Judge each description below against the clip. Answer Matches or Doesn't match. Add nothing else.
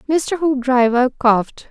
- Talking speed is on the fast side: Doesn't match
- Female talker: Matches